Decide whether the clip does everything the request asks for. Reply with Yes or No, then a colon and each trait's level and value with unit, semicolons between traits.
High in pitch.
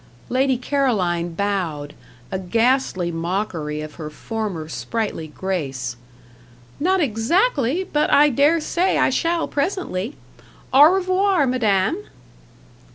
Yes: high, 225 Hz